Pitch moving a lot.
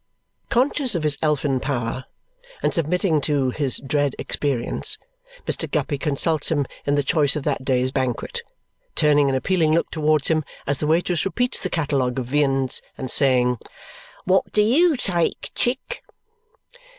No: average, 3.9 semitones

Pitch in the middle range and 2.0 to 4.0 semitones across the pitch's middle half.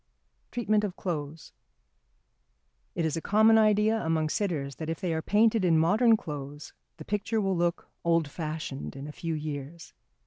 No: medium, 165 Hz; average, 5.3 semitones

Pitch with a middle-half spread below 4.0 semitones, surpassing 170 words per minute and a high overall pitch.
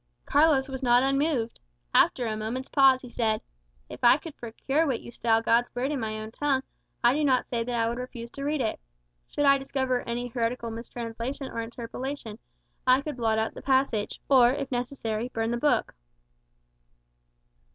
Yes: average, 2.8 semitones; average, 185 wpm; high, 245 Hz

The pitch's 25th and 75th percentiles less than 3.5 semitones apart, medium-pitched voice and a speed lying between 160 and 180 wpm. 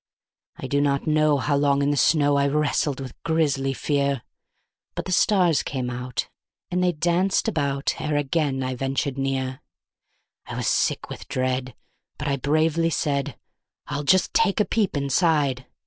Yes: narrow, 2.6 semitones; medium, 145 Hz; average, 165 wpm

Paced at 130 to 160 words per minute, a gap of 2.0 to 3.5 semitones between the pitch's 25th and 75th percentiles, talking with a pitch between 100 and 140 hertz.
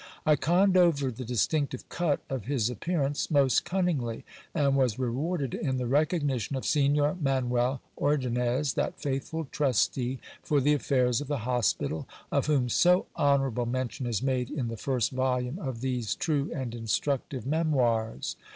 Yes: average, 150 wpm; average, 3.0 semitones; low, 135 Hz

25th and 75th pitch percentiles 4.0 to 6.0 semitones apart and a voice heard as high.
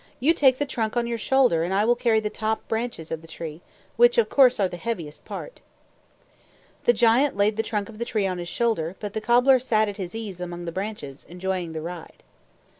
Yes: average, 5.2 semitones; high, 215 Hz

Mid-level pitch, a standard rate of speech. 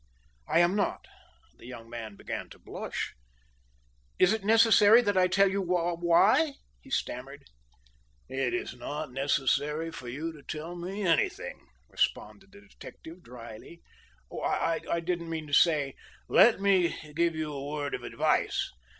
Yes: medium, 165 Hz; average, 150 wpm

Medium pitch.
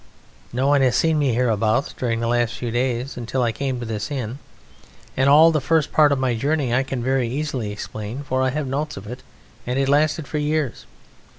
No: low, 130 Hz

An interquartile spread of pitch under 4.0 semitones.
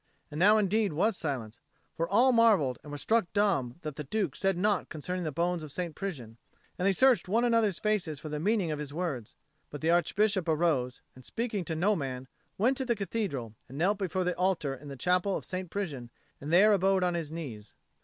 No: wide, 5.6 semitones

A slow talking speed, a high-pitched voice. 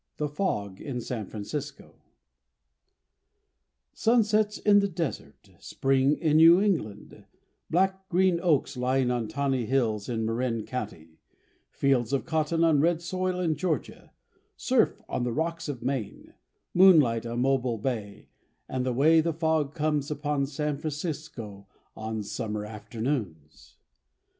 No: slow, 130 wpm; medium, 140 Hz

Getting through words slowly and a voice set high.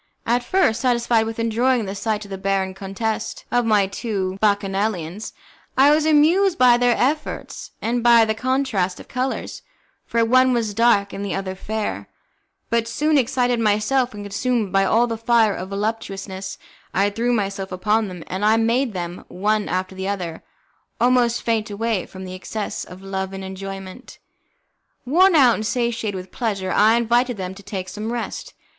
No: average, 175 wpm; high, 220 Hz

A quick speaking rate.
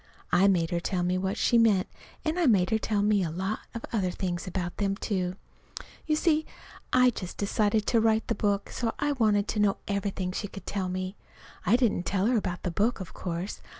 Yes: fast, 215 wpm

